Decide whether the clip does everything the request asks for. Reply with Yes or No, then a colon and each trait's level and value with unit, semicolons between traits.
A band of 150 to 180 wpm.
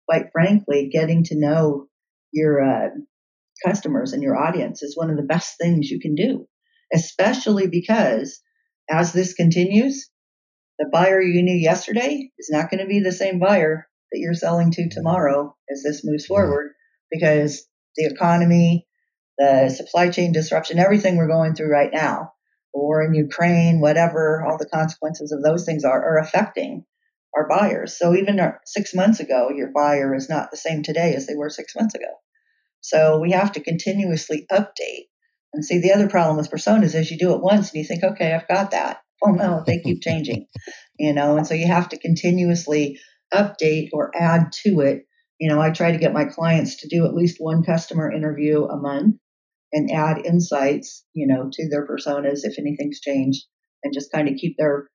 No: average, 190 wpm